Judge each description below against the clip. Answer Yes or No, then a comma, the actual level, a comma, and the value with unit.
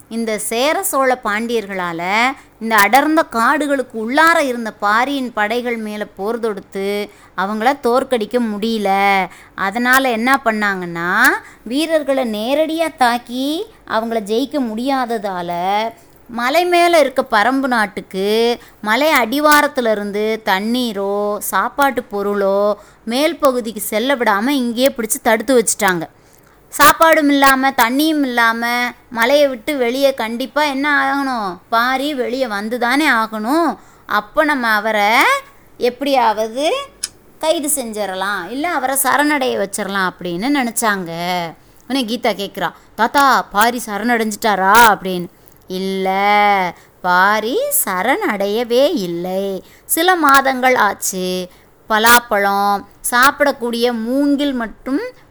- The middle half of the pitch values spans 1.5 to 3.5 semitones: No, average, 5.0 semitones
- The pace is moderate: Yes, average, 95 wpm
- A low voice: No, high, 235 Hz